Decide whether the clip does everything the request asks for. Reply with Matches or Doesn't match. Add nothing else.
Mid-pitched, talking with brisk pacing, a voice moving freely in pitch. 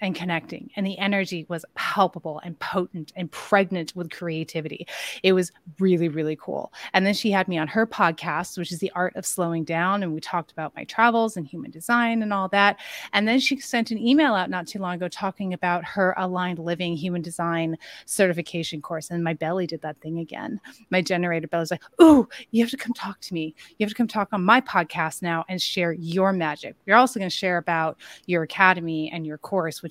Doesn't match